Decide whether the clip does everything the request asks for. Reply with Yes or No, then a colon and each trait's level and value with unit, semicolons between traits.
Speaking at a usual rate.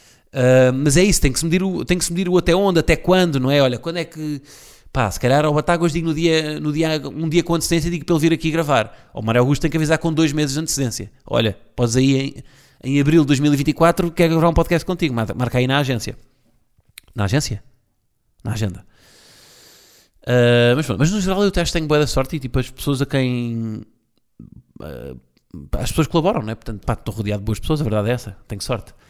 No: fast, 235 wpm